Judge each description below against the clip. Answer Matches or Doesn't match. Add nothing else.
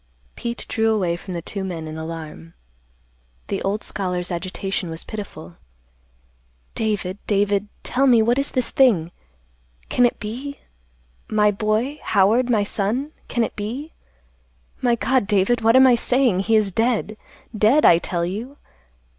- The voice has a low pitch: Doesn't match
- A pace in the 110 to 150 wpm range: Matches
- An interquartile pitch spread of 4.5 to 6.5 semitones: Matches